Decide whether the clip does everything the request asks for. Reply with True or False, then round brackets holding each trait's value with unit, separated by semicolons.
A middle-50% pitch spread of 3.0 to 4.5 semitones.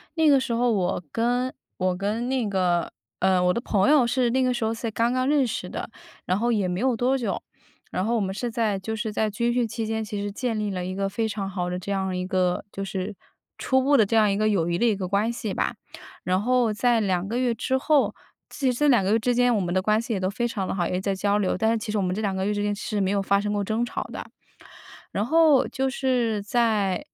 True (3.7 semitones)